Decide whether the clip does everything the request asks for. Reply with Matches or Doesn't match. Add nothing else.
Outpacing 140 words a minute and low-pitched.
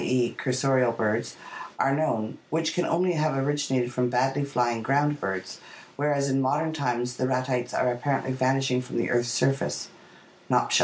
Matches